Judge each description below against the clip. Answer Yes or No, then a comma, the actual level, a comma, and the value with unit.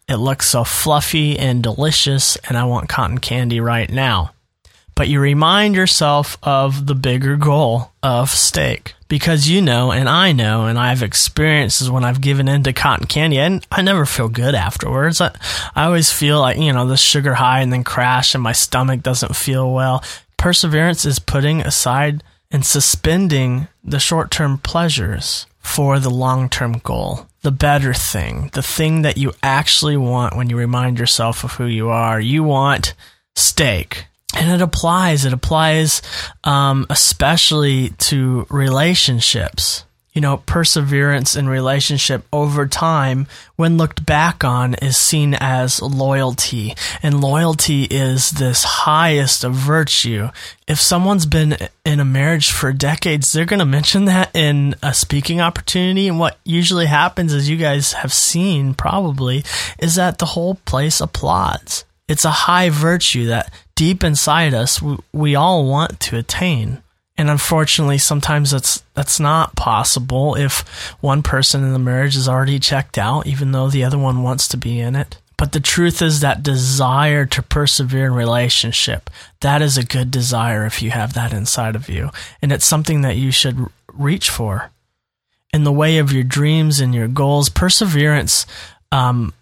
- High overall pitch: No, medium, 140 Hz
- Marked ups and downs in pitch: No, average, 3.3 semitones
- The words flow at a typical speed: Yes, average, 165 wpm